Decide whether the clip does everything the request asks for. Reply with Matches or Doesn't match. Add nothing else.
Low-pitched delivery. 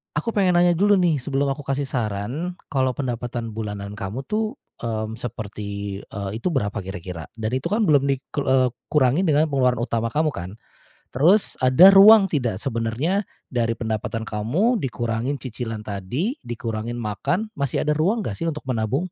Matches